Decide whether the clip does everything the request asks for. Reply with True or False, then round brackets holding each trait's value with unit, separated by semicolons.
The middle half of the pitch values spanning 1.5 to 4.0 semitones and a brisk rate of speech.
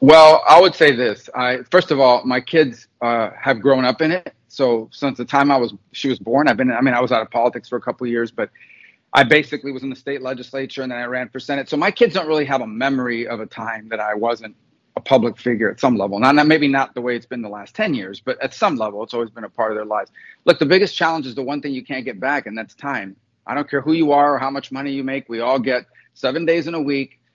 True (3.3 semitones; 290 wpm)